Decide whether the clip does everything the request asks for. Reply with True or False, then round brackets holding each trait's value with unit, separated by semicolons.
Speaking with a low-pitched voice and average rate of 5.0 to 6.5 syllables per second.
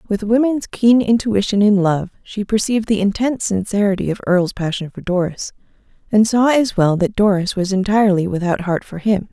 False (200 Hz; 5.5 syllables/s)